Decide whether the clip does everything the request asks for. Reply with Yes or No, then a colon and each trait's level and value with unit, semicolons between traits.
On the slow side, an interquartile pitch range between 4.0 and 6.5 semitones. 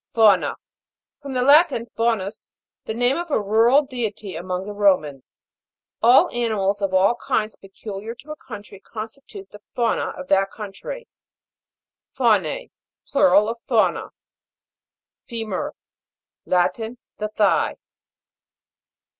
No: slow, 120 wpm; average, 3.6 semitones